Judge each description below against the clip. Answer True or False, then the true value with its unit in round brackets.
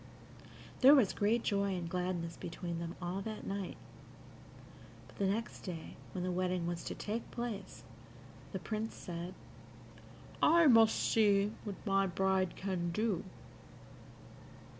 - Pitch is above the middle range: True (195 Hz)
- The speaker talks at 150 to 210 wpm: False (135 wpm)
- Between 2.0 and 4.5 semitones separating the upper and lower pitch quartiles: True (3.3 semitones)